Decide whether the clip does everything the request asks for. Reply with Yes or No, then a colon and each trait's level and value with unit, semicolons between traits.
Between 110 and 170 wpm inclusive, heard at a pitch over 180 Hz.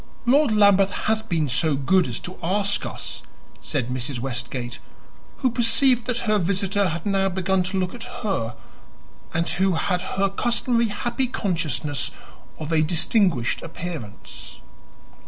Yes: average, 140 wpm; high, 190 Hz